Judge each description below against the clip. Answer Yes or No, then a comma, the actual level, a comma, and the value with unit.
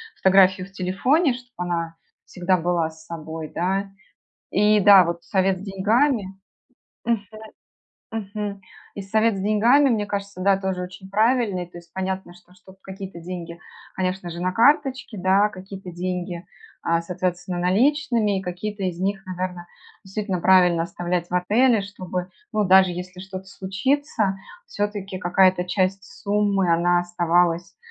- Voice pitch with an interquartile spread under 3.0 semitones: Yes, narrow, 2.4 semitones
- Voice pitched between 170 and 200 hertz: Yes, high, 190 Hz